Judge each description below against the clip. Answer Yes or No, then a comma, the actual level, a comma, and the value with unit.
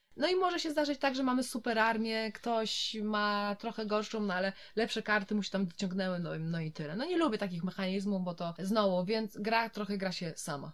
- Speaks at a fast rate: Yes, fast, 230 wpm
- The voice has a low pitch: No, high, 210 Hz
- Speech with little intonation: No, average, 3.1 semitones